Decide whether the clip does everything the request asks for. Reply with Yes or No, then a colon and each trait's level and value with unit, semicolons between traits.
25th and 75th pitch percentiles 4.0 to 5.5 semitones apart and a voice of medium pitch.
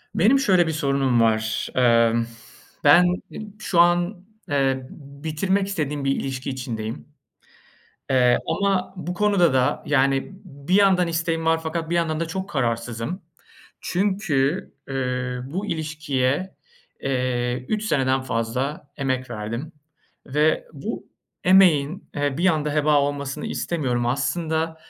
Yes: average, 5.0 semitones; medium, 145 Hz